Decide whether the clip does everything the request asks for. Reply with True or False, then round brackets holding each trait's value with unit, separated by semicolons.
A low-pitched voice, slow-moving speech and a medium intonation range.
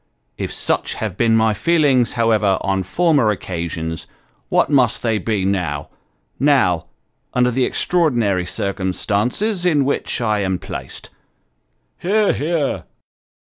False (115 Hz; 120 wpm; 6.7 semitones)